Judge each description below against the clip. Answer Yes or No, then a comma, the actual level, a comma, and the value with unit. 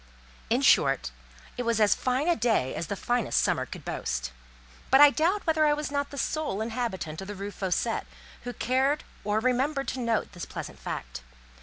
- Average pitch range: No, wide, 5.9 semitones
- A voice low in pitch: No, high, 240 Hz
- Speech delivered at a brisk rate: No, average, 190 wpm